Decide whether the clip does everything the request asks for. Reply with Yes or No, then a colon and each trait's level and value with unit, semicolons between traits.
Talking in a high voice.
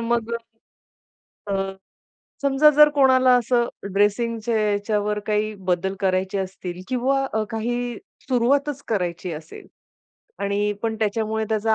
Yes: high, 220 Hz